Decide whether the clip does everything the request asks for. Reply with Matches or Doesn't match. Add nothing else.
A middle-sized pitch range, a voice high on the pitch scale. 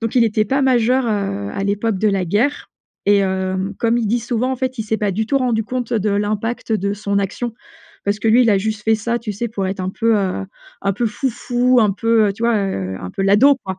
Matches